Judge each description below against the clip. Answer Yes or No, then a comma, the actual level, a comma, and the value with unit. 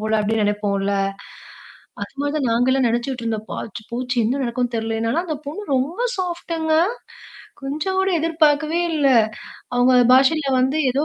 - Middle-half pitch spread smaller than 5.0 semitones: No, average, 5.3 semitones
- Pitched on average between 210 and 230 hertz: No, very high, 260 Hz